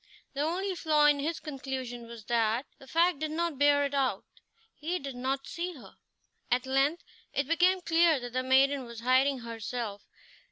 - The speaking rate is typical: Yes, average, 175 wpm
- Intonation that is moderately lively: Yes, average, 3.9 semitones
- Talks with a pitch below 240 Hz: No, very high, 275 Hz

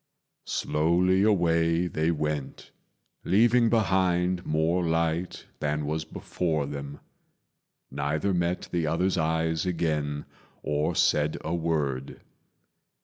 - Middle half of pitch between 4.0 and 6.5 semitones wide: No, average, 2.8 semitones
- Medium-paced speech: No, slow, 100 wpm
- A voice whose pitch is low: Yes, very low, 80 Hz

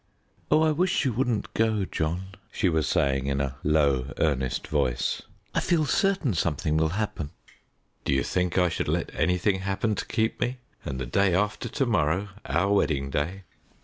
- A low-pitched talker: Yes, very low, 90 Hz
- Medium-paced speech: Yes, average, 180 wpm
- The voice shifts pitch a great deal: Yes, wide, 7.1 semitones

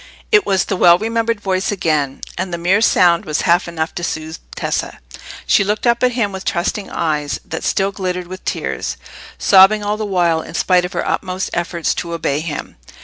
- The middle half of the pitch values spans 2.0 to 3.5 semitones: Yes, average, 3.2 semitones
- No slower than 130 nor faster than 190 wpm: No, average, 200 wpm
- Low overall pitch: No, medium, 185 Hz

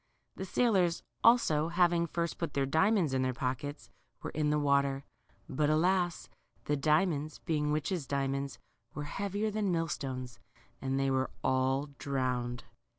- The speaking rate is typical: Yes, average, 150 wpm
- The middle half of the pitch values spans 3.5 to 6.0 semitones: Yes, average, 4.1 semitones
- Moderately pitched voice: Yes, medium, 150 Hz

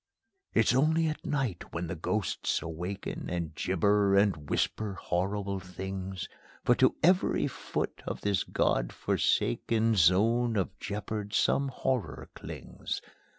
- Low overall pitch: Yes, low, 100 Hz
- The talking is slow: Yes, slow, 125 wpm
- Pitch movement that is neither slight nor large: Yes, average, 3.9 semitones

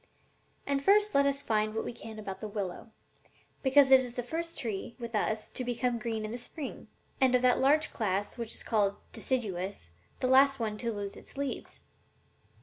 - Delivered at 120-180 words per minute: No, average, 200 wpm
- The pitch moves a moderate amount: Yes, average, 3.9 semitones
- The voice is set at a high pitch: Yes, high, 235 Hz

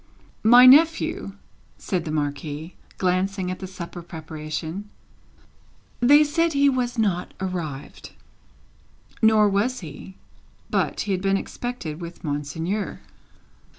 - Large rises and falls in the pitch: Yes, wide, 6.8 semitones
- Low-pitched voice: No, high, 190 Hz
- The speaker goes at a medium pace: No, slow, 115 wpm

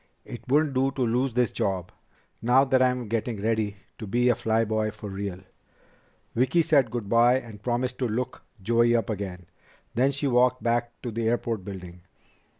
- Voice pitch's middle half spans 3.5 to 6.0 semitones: No, average, 2.8 semitones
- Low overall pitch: Yes, low, 120 Hz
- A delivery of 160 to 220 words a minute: Yes, average, 180 wpm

